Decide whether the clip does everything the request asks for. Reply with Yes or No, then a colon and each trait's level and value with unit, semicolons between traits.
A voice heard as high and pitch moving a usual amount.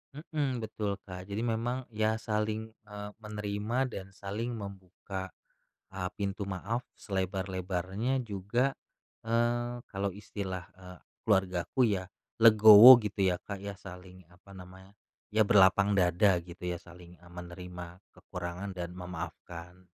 No: low, 100 Hz; average, 3.0 semitones